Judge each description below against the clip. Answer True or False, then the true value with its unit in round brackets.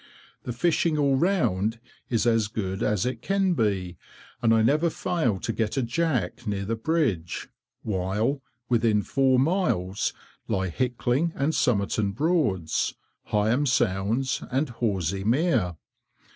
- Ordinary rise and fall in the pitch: False (5.8 semitones)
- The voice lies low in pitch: True (115 Hz)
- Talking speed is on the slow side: True (130 wpm)